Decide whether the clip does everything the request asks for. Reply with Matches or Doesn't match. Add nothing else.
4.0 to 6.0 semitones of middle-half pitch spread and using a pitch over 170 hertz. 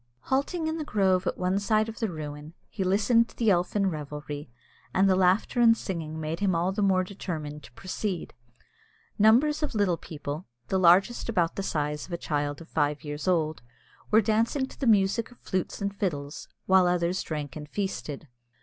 Matches